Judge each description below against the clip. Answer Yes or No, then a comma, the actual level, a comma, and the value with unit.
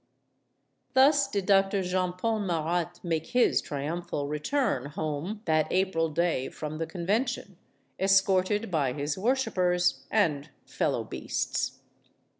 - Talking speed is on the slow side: Yes, slow, 120 wpm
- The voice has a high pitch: No, medium, 180 Hz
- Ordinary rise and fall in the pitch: Yes, average, 4.4 semitones